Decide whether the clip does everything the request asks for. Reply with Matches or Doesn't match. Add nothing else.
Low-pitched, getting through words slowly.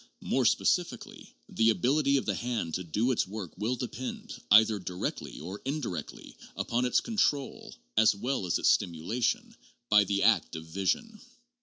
Doesn't match